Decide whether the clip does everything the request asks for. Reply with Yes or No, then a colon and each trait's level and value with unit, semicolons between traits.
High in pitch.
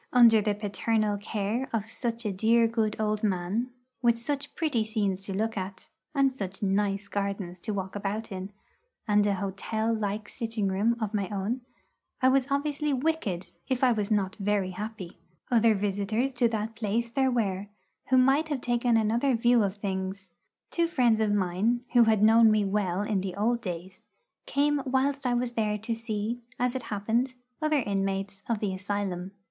Yes: high, 215 Hz